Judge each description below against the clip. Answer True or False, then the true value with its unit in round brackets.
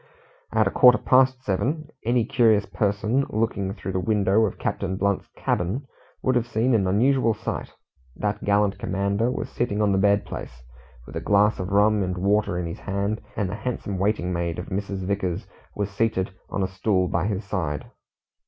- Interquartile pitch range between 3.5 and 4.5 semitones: False (2.8 semitones)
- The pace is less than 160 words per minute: False (185 wpm)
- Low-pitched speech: True (100 Hz)